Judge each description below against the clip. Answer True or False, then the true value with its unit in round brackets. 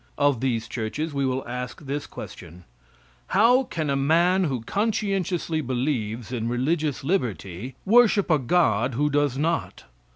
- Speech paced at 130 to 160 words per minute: True (140 wpm)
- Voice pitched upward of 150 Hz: False (140 Hz)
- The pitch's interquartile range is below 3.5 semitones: False (5.6 semitones)